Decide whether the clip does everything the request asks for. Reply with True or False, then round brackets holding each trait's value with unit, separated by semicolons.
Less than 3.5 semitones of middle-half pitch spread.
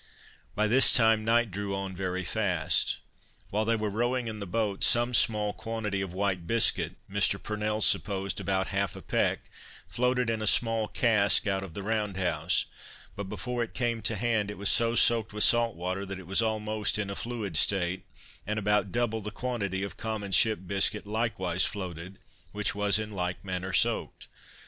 True (2.6 semitones)